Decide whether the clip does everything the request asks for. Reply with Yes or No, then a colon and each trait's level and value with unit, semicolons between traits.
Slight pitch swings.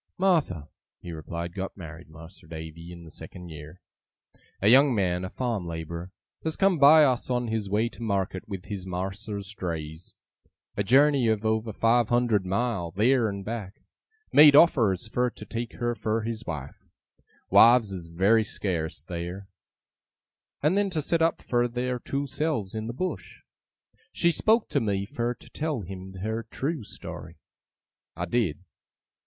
No: wide, 5.4 semitones